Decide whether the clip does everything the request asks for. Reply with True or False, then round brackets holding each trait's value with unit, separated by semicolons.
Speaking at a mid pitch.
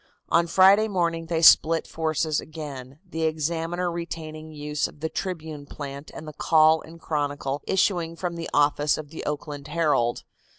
True (160 Hz)